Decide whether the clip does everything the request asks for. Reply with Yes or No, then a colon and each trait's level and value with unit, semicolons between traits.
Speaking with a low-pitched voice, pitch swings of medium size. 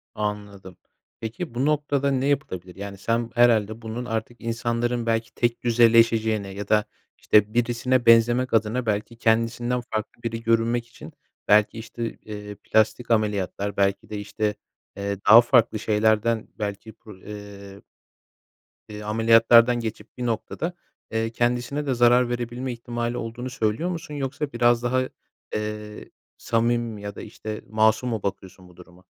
No: low, 115 Hz; narrow, 2.2 semitones